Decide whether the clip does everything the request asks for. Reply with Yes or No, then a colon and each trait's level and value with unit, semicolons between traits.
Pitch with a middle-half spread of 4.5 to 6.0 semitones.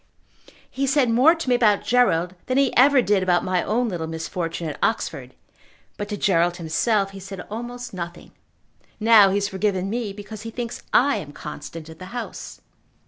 Yes: wide, 5.4 semitones